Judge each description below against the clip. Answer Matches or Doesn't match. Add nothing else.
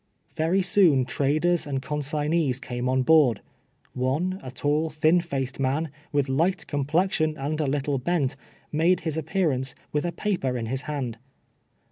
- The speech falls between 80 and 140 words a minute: Doesn't match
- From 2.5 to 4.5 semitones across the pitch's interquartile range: Matches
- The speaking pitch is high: Doesn't match